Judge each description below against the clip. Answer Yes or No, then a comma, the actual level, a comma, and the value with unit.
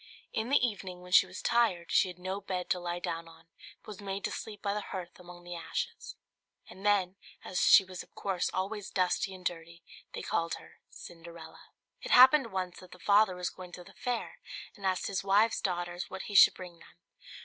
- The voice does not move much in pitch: Yes, narrow, 2.3 semitones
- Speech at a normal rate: No, fast, 215 wpm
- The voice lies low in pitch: No, medium, 185 Hz